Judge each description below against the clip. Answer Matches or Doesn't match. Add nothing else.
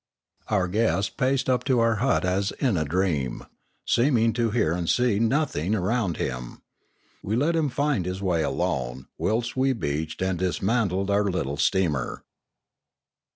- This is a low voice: Matches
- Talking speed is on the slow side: Doesn't match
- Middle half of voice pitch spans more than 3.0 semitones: Matches